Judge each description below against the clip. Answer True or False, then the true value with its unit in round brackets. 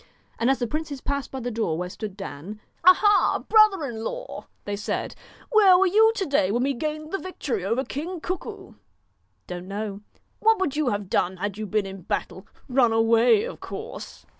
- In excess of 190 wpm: True (200 wpm)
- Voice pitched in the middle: False (250 Hz)